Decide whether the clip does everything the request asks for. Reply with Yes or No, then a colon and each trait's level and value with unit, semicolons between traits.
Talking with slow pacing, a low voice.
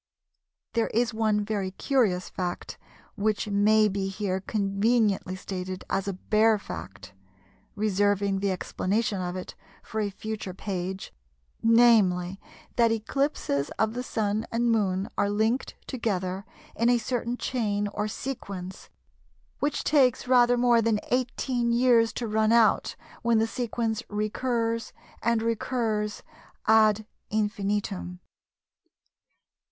No: slow, 120 wpm; high, 215 Hz